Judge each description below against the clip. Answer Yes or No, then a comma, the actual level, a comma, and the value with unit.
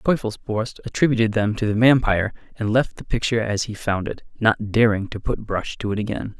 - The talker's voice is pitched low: Yes, low, 110 Hz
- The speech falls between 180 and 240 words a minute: Yes, fast, 205 wpm